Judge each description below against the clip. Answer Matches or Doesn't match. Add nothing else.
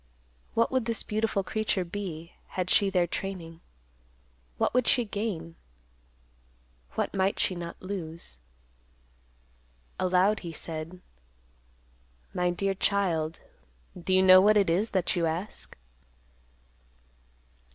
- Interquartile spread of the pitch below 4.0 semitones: Matches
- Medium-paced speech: Doesn't match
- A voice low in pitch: Doesn't match